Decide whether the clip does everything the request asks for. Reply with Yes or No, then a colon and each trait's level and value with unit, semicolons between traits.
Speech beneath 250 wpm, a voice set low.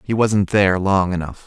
Yes: fast, 205 wpm; low, 100 Hz